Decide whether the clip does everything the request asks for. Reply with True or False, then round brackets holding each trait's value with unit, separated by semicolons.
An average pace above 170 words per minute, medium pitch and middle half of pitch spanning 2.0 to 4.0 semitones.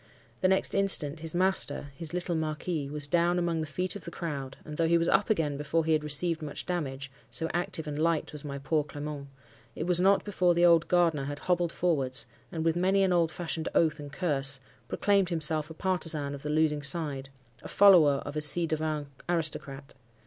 True (190 wpm; 160 Hz; 3.2 semitones)